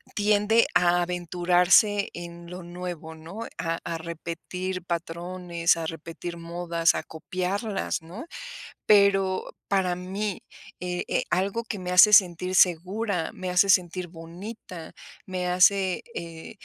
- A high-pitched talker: No, medium, 180 Hz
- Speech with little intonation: Yes, narrow, 2.1 semitones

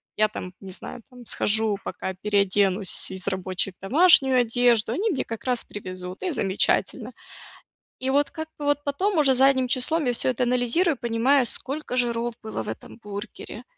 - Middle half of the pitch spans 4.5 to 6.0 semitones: Yes, average, 5.0 semitones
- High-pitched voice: Yes, high, 240 Hz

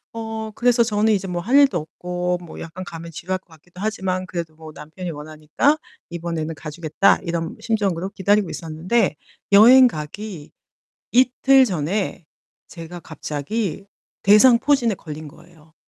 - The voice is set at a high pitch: No, medium, 180 Hz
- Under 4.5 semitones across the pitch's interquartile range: No, average, 5.1 semitones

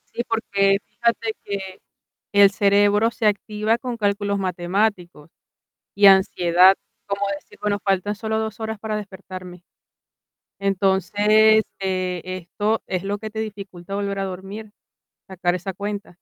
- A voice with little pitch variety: Yes, narrow, 2.0 semitones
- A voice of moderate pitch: No, high, 200 Hz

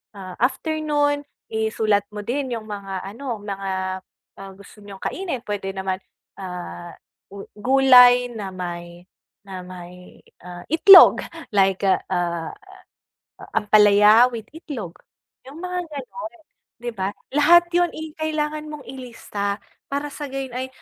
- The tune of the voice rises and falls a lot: Yes, wide, 6.8 semitones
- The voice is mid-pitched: No, high, 220 Hz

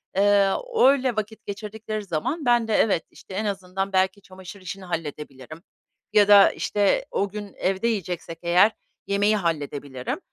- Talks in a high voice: Yes, high, 195 Hz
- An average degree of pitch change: Yes, average, 3.1 semitones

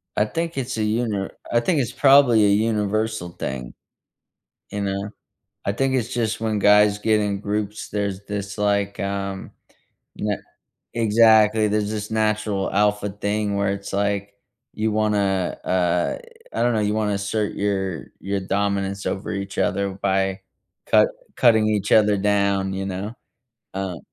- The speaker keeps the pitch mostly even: Yes, narrow, 1.6 semitones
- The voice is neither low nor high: No, low, 105 Hz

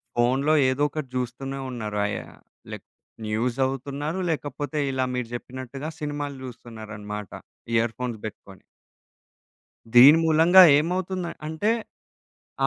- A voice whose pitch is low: Yes, low, 130 Hz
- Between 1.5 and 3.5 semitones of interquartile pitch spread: No, average, 4.0 semitones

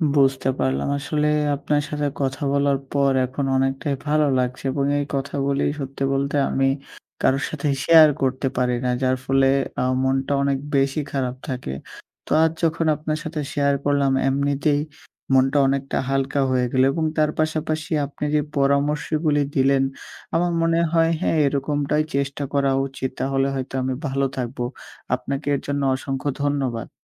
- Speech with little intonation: Yes, narrow, 1.7 semitones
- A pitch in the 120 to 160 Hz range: Yes, medium, 140 Hz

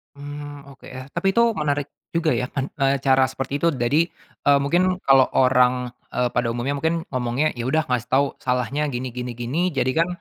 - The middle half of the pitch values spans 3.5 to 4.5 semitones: No, average, 2.9 semitones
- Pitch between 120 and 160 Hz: Yes, low, 135 Hz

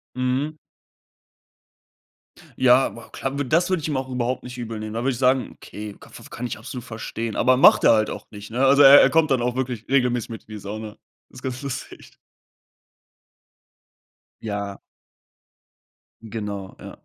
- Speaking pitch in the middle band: No, low, 125 Hz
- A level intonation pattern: No, average, 3.1 semitones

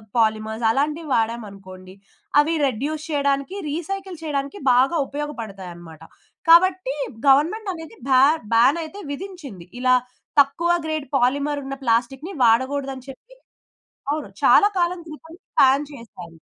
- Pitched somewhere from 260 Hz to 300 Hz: Yes, very high, 275 Hz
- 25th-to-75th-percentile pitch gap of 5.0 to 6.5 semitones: Yes, wide, 5.4 semitones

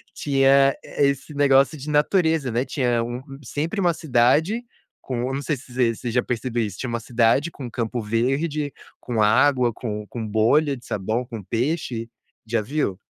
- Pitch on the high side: No, low, 125 Hz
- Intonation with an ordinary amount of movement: Yes, average, 3.8 semitones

